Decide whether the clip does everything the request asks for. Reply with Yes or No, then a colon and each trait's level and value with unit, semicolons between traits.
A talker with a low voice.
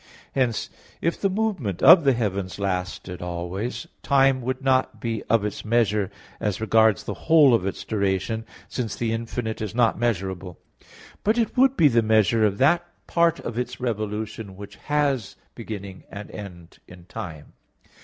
Yes: low, 110 Hz